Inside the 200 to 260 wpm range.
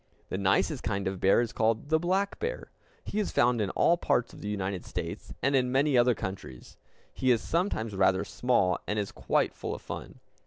Yes: fast, 205 wpm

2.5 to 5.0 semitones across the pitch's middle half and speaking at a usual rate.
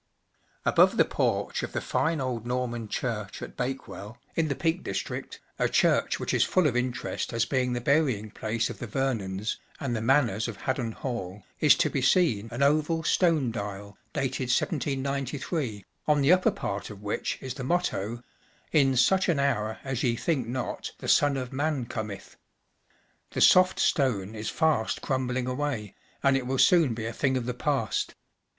Yes: average, 3.9 semitones; average, 190 wpm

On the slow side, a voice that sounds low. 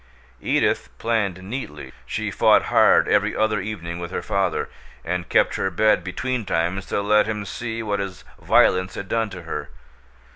No: average, 160 wpm; low, 100 Hz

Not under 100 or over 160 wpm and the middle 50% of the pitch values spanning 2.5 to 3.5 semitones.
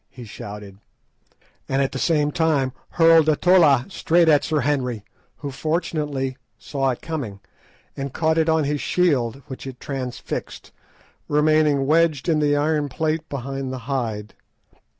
Yes: average, 150 wpm; average, 3.2 semitones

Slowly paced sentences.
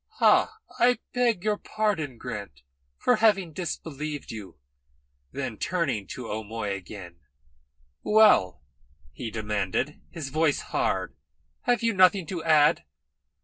Yes: slow, 115 wpm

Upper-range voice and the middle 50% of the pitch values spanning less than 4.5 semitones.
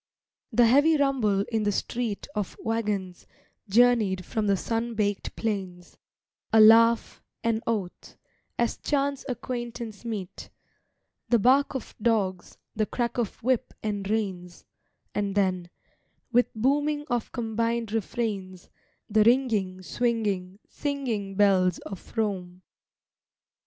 Yes: high, 220 Hz; average, 3.4 semitones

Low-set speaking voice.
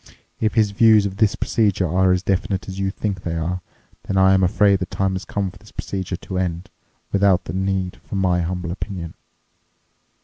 Yes: very low, 95 Hz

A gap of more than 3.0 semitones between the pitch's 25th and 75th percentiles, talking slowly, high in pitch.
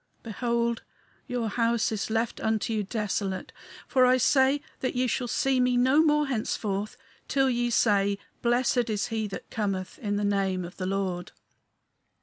No: average, 3.6 semitones; average, 160 wpm; high, 225 Hz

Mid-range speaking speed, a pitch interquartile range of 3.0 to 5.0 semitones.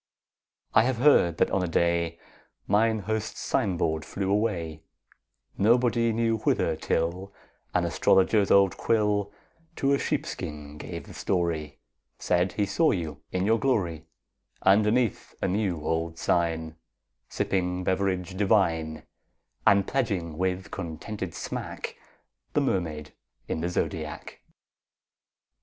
No: slow, 125 wpm; average, 4.2 semitones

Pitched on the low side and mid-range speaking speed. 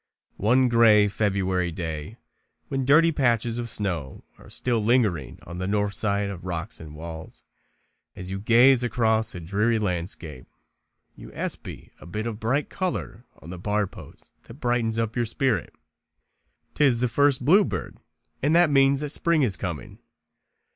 Yes: low, 110 Hz; average, 155 wpm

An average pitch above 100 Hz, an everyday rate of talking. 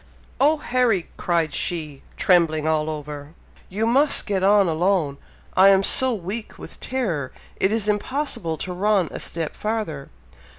Yes: medium, 185 Hz; average, 145 wpm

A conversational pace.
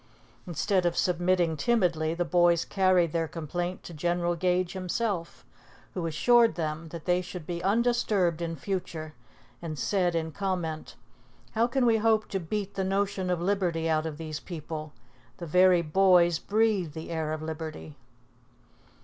Yes: average, 155 wpm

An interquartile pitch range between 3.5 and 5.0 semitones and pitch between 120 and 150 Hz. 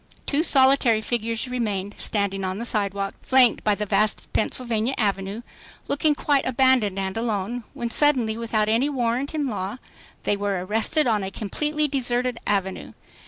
No: average, 4.2 semitones; high, 230 Hz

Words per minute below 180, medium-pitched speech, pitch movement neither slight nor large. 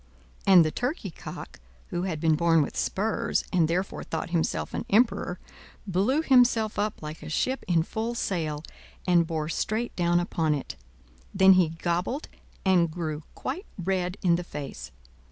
Yes: average, 160 wpm; medium, 175 Hz; average, 4.0 semitones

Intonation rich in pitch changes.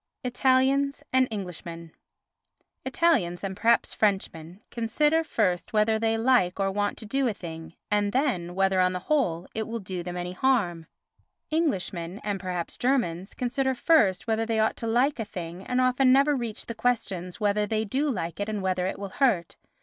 Yes: wide, 5.7 semitones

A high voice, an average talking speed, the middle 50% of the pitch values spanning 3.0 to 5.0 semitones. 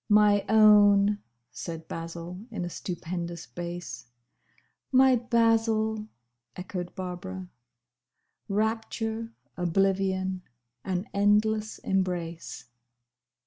No: high, 195 Hz; slow, 75 wpm; average, 3.5 semitones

